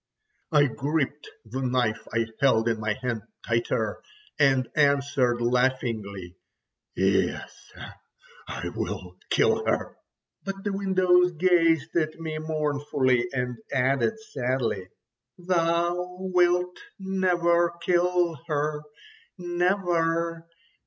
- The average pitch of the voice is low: No, medium, 155 Hz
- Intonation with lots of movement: Yes, wide, 5.8 semitones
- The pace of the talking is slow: Yes, slow, 100 wpm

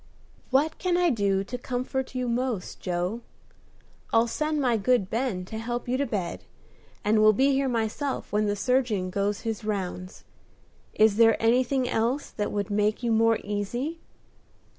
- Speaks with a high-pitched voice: Yes, high, 225 Hz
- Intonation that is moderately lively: Yes, average, 3.8 semitones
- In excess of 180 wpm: No, average, 160 wpm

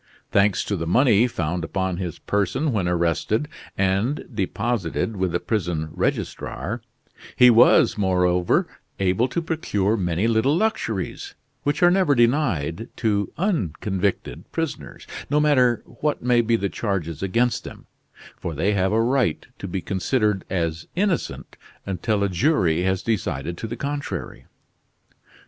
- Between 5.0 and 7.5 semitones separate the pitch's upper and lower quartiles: Yes, wide, 5.4 semitones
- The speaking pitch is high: No, low, 105 Hz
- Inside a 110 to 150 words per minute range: Yes, average, 140 wpm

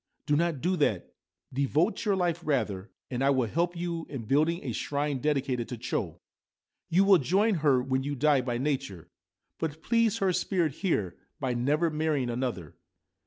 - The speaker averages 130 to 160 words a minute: No, average, 180 wpm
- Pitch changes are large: No, average, 4.9 semitones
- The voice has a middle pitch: Yes, medium, 145 Hz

